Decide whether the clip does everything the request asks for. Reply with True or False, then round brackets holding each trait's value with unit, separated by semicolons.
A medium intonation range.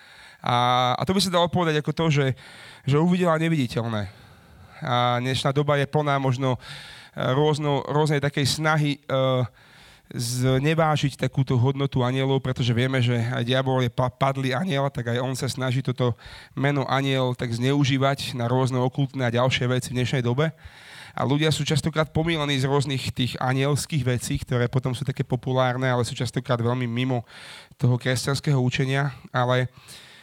False (2.3 semitones)